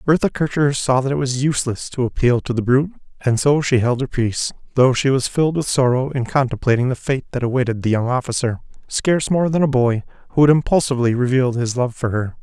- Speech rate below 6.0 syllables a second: No, 6.2 syllables/s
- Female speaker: No, male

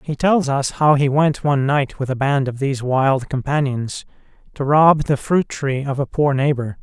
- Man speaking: Yes, male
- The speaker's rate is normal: No, fast, 210 wpm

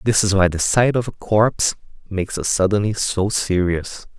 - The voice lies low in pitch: Yes, low, 100 Hz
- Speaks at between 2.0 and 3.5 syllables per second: No, 4.8 syllables/s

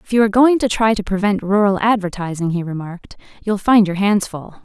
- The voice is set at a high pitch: Yes, high, 200 Hz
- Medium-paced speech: No, fast, 220 wpm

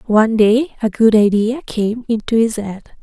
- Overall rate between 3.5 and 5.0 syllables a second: Yes, 4.6 syllables/s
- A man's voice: No, female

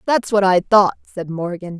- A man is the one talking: No, female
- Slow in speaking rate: No, average, 200 wpm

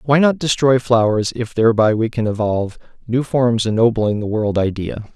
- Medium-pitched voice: No, low, 115 Hz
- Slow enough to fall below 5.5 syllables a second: Yes, 5.0 syllables/s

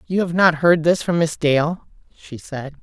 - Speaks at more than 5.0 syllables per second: No, 4.4 syllables/s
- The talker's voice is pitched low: No, medium, 160 Hz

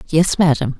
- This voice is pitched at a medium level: Yes, medium, 155 Hz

